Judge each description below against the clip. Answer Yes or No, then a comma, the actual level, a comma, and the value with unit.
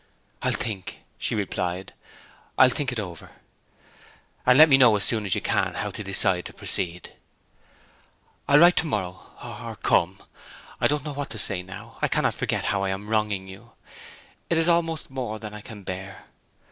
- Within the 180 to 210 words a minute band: Yes, average, 190 wpm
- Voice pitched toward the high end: No, low, 105 Hz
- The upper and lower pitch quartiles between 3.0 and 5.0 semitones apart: No, wide, 5.6 semitones